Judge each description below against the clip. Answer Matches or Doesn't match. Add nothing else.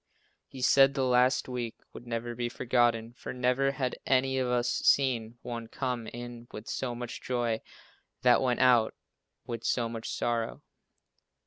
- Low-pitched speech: Matches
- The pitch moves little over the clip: Matches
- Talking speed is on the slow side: Doesn't match